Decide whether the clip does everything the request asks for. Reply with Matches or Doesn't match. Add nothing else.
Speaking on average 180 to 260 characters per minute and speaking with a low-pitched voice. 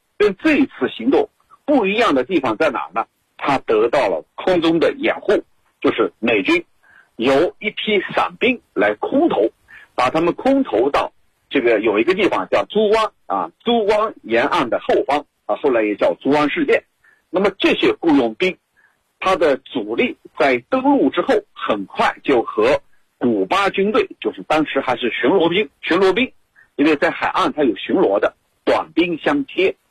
Doesn't match